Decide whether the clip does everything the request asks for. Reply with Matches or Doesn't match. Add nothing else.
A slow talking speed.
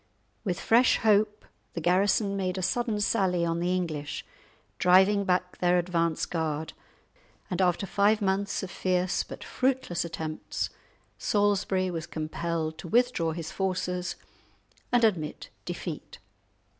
Matches